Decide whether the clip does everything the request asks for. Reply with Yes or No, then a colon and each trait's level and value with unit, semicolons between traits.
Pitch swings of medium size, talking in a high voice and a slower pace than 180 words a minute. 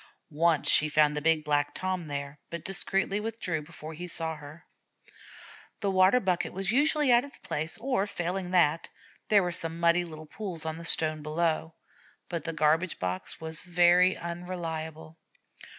No: average, 3.0 semitones; medium, 170 Hz; average, 165 wpm